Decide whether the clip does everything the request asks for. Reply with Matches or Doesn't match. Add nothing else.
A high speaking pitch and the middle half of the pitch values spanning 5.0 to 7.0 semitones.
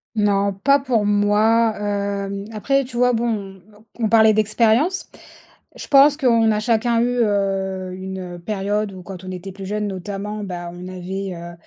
Doesn't match